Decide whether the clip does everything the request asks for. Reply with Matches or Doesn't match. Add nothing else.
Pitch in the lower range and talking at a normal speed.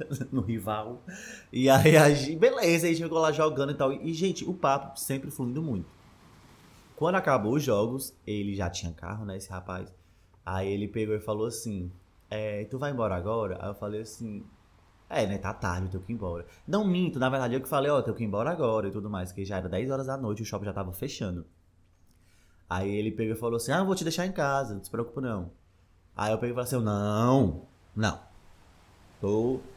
Doesn't match